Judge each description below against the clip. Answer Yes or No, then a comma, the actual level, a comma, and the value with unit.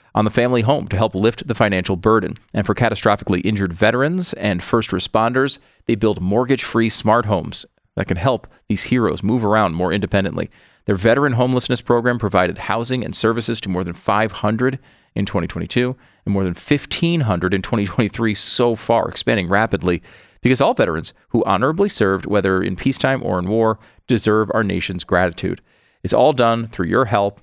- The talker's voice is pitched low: Yes, low, 110 Hz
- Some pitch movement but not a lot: Yes, average, 3.6 semitones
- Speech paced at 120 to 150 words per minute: No, average, 175 wpm